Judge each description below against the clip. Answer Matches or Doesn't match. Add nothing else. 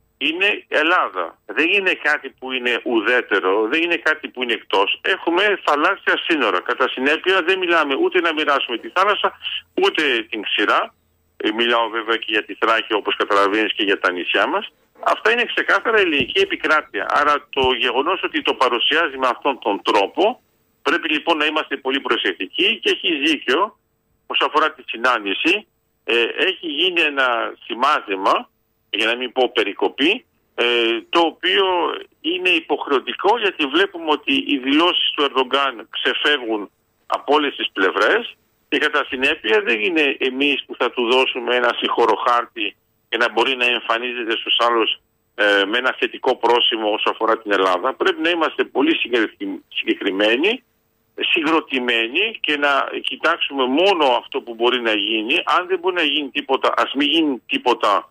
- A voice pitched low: Doesn't match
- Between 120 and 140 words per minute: Doesn't match